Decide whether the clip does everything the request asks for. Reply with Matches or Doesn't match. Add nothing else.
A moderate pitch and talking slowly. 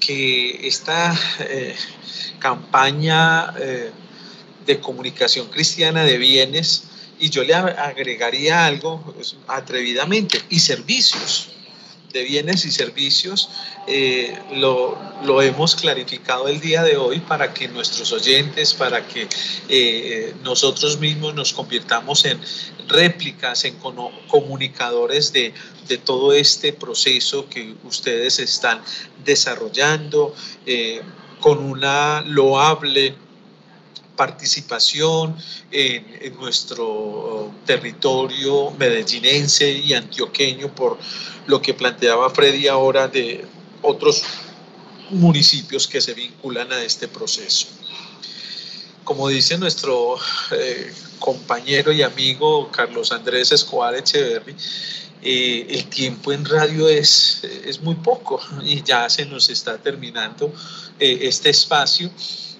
Matches